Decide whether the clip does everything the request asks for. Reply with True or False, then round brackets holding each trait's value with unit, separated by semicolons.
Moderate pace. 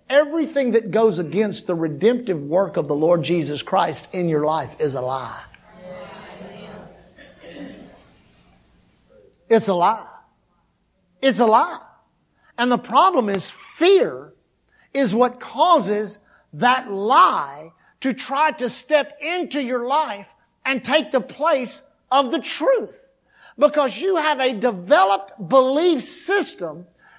False (120 wpm)